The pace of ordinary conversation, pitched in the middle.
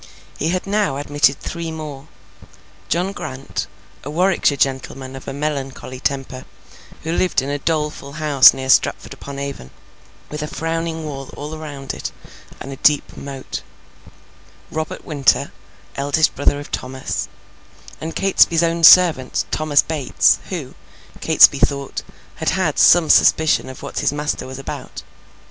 Yes: average, 145 wpm; medium, 145 Hz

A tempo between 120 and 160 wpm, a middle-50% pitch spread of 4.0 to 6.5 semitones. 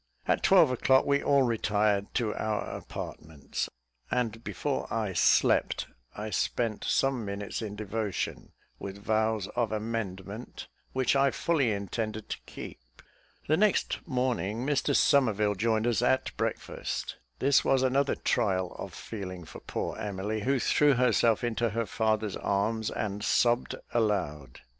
No: average, 140 wpm; average, 3.5 semitones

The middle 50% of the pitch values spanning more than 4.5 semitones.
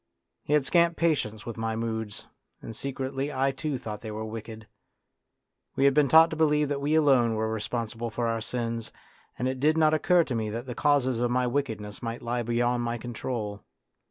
No: average, 3.8 semitones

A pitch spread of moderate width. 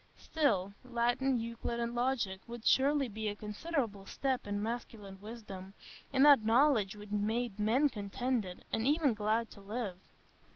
Yes: average, 3.7 semitones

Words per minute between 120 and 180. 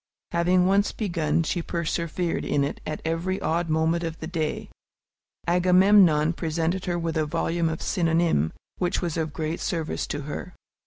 Yes: average, 160 wpm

